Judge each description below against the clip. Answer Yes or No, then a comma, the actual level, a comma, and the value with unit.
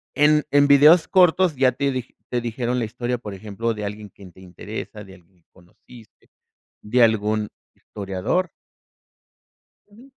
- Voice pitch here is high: No, low, 115 Hz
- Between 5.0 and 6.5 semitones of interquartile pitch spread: Yes, average, 5.3 semitones